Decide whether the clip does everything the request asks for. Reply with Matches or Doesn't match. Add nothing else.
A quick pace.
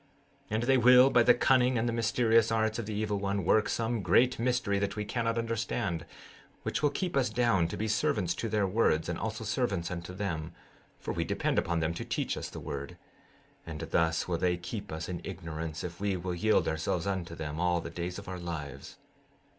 Matches